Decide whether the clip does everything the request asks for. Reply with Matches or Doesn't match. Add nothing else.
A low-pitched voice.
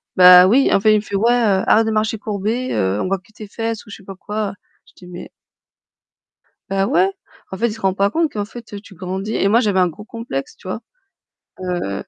Doesn't match